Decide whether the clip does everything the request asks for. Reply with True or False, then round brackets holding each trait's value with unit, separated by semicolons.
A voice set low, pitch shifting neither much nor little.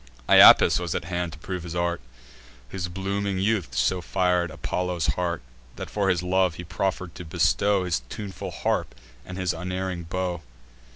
False (90 Hz; 1.5 semitones)